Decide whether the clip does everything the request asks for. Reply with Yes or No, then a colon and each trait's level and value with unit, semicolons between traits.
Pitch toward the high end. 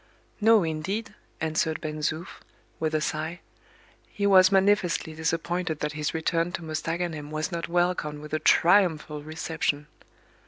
No: medium, 160 Hz